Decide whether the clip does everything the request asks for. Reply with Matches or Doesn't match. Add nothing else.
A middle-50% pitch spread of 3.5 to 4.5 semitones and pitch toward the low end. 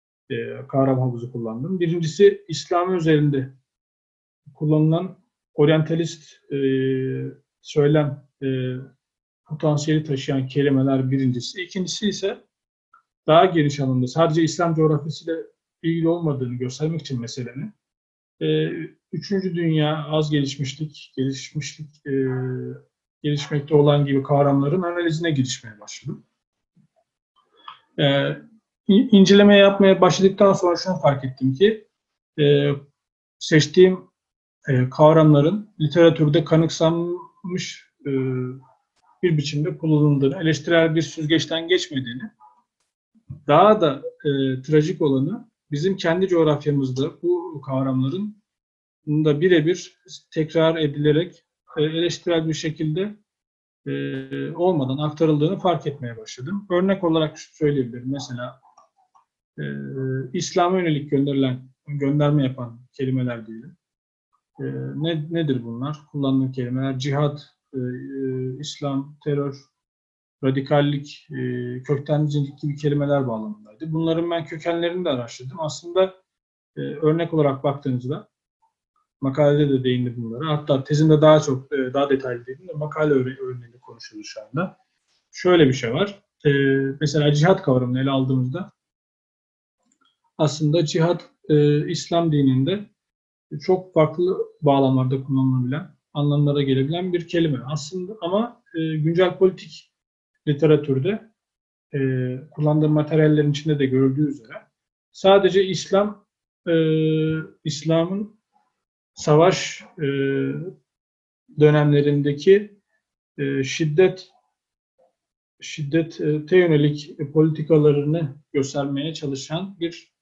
Doesn't match